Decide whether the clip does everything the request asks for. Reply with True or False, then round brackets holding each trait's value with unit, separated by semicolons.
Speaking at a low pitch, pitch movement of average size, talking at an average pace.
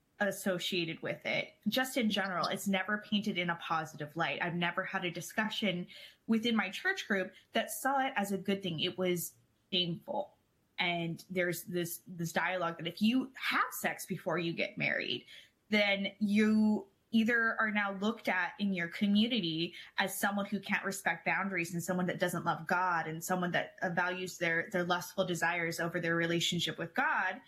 False (185 Hz; 3.3 semitones; 175 wpm)